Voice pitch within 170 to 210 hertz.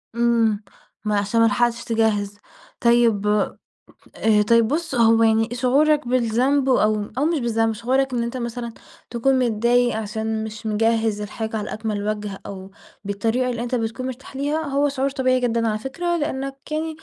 No: high, 235 Hz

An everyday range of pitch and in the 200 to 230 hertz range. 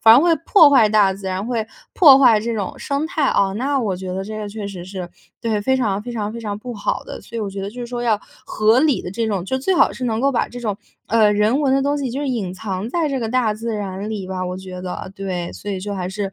Yes: average, 4.2 semitones; high, 215 Hz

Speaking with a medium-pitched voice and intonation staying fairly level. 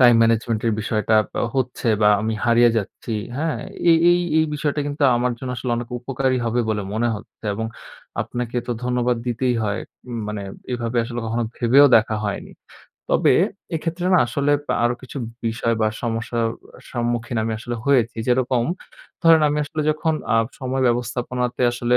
No: low, 120 Hz; narrow, 2.3 semitones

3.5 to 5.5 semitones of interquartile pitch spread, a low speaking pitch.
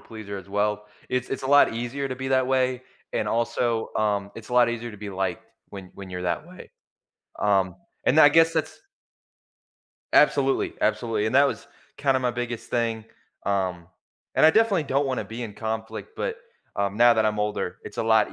Yes: average, 4.2 semitones; low, 115 Hz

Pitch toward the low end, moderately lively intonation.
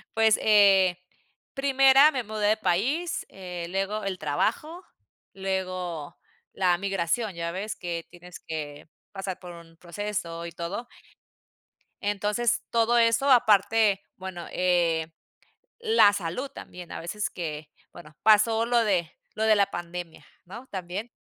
No: high, 195 Hz; average, 4.1 semitones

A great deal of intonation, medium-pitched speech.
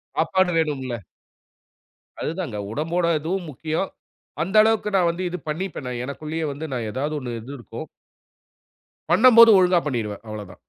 Yes: wide, 5.7 semitones; medium, 160 Hz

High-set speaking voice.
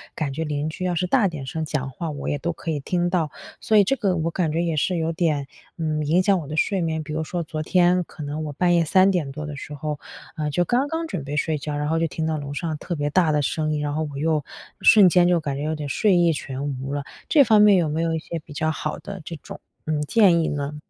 No: medium, 160 Hz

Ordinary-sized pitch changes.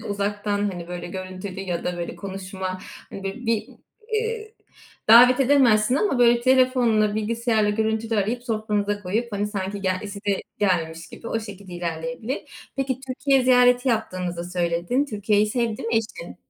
Yes: average, 4.2 semitones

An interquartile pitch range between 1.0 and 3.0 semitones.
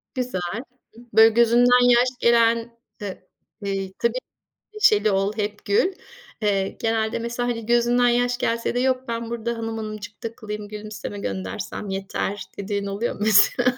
Yes: narrow, 2.6 semitones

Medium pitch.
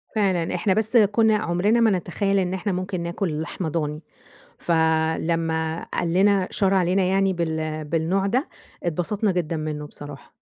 Yes: medium, 180 Hz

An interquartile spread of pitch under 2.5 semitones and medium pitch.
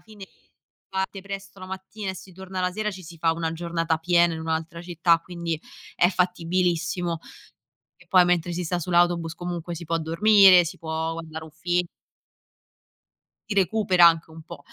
Yes: narrow, 2.0 semitones; medium, 175 Hz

